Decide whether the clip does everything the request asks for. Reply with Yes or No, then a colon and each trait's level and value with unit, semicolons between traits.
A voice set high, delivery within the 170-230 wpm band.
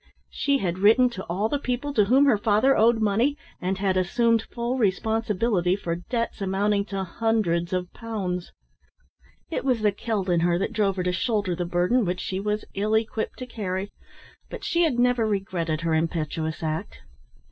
Yes: high, 205 Hz; average, 180 wpm